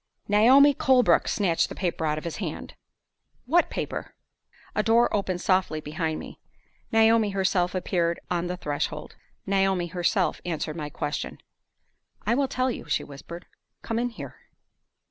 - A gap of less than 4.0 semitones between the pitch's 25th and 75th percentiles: No, average, 4.9 semitones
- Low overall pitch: No, medium, 185 Hz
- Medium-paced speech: Yes, average, 145 wpm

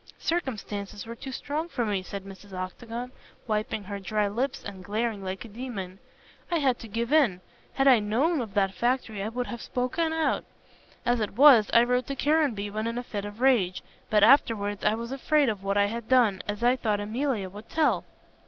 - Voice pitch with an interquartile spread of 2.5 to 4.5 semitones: Yes, average, 4.0 semitones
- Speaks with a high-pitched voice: Yes, high, 225 Hz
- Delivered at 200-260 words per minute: Yes, fast, 205 wpm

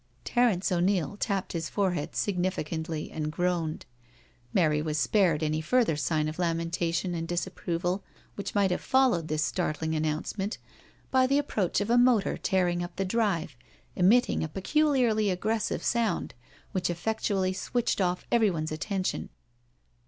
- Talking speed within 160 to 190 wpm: No, average, 145 wpm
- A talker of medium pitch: Yes, medium, 180 Hz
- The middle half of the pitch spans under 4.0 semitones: No, average, 4.3 semitones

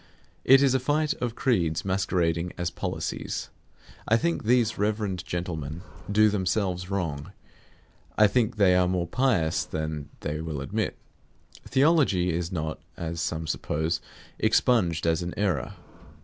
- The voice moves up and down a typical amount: Yes, average, 4.7 semitones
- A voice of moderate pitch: No, very low, 90 Hz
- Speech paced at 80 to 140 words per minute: Yes, slow, 135 wpm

